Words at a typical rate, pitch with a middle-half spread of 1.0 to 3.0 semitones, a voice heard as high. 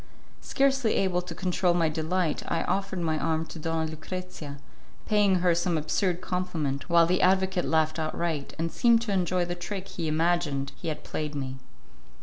No: average, 170 wpm; average, 2.7 semitones; medium, 170 Hz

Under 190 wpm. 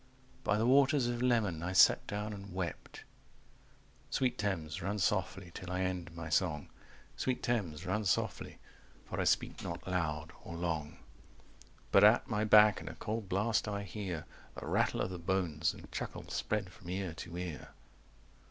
Yes: average, 170 wpm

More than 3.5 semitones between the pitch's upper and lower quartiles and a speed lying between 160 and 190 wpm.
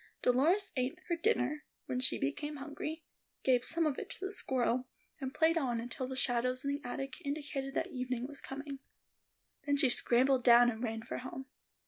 No: average, 2.9 semitones; average, 185 wpm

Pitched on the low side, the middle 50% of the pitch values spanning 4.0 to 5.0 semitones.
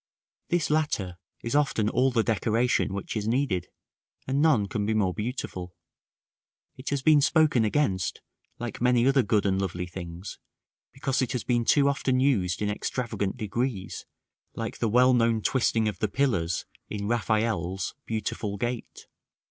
Yes: low, 115 Hz; average, 4.5 semitones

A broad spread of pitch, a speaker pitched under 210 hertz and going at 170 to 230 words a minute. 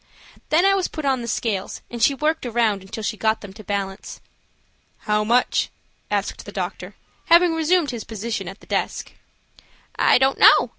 No: wide, 6.3 semitones; high, 235 Hz; average, 180 wpm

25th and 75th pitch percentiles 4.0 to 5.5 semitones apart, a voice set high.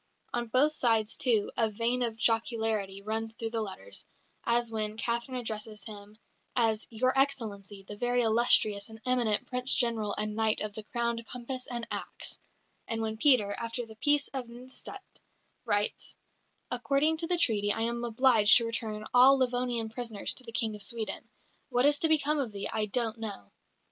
No: narrow, 2.5 semitones; high, 230 Hz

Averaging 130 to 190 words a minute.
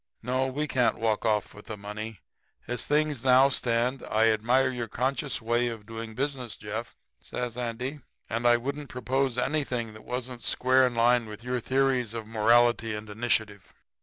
Yes: average, 170 wpm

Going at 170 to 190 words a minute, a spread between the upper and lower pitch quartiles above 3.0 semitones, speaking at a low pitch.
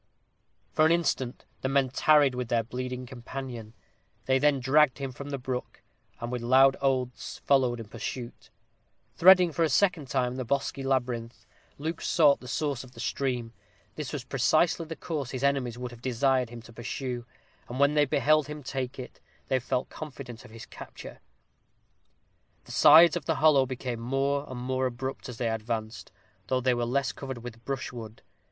No: average, 180 wpm; narrow, 2.5 semitones; low, 130 Hz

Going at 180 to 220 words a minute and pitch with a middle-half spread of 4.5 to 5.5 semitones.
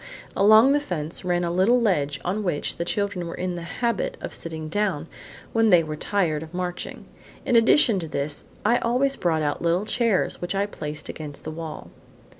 Yes: average, 195 wpm; average, 5.0 semitones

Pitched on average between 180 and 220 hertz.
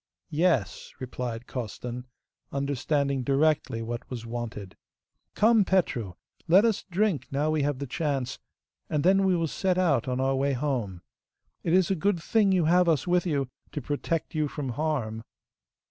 No: medium, 145 Hz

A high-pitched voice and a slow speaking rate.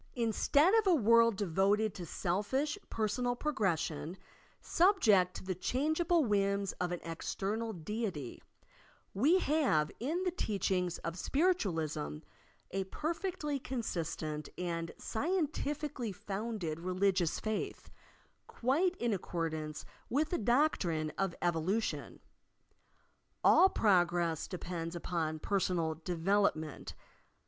Yes: high, 200 Hz; slow, 105 wpm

